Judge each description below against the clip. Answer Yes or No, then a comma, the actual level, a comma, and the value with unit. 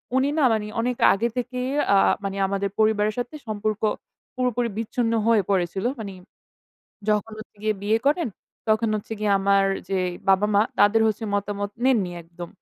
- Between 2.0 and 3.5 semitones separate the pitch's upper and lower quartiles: Yes, narrow, 2.6 semitones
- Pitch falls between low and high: No, high, 215 Hz